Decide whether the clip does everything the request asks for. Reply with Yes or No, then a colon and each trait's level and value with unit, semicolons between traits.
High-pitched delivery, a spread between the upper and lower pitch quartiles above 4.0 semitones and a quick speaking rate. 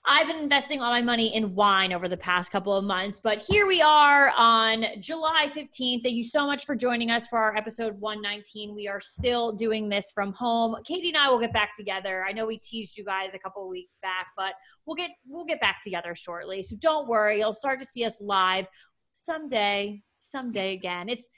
Yes: high, 220 Hz; average, 4.7 semitones; fast, 220 wpm